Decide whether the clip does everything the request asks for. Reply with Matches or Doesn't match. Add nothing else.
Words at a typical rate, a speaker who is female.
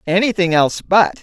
Matches